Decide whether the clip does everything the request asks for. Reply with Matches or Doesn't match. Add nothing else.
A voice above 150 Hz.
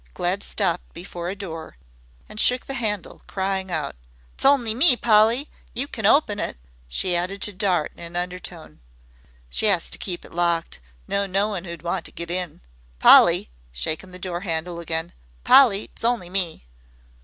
Matches